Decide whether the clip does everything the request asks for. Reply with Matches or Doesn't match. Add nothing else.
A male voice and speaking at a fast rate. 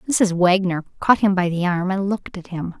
Doesn't match